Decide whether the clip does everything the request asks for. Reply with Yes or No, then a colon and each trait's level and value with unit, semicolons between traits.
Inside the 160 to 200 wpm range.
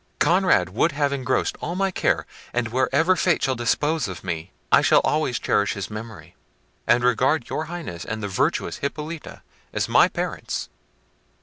Yes: average, 165 wpm